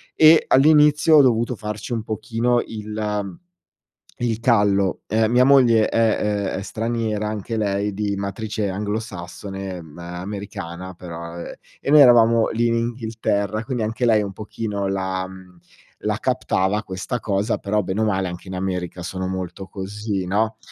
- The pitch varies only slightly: No, average, 3.1 semitones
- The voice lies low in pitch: Yes, low, 105 Hz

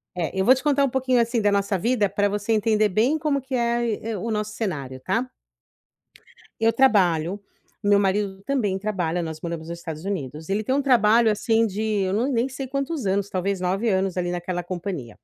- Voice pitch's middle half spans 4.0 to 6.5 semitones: Yes, average, 4.4 semitones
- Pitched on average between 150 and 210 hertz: Yes, high, 205 Hz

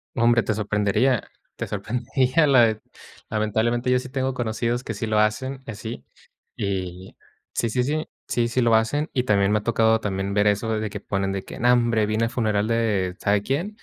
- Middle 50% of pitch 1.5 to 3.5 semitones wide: Yes, average, 2.9 semitones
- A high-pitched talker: No, low, 110 Hz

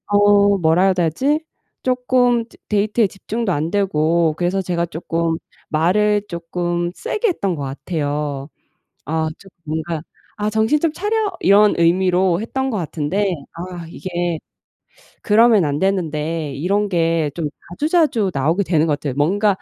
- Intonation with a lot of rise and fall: No, average, 4.4 semitones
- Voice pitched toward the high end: No, medium, 180 Hz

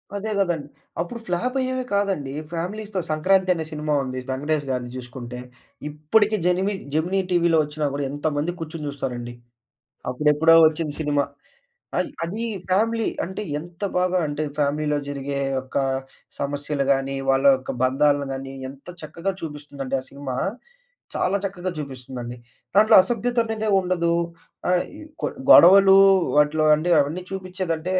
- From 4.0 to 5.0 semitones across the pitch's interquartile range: Yes, average, 4.7 semitones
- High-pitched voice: No, medium, 155 Hz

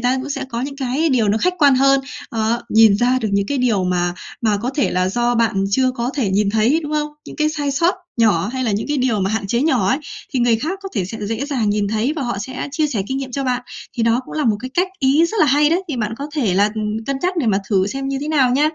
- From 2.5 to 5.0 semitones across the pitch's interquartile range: Yes, average, 4.7 semitones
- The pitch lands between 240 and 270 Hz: Yes, high, 245 Hz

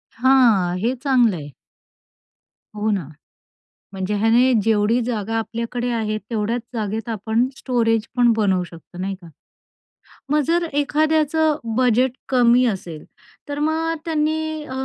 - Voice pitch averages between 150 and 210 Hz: No, high, 235 Hz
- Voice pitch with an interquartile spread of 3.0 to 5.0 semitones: Yes, average, 4.5 semitones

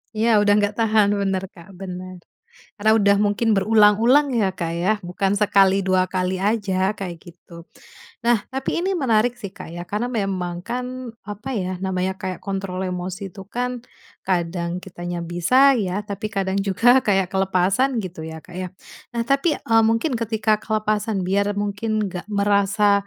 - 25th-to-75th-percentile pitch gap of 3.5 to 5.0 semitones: No, average, 3.0 semitones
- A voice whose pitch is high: Yes, high, 200 Hz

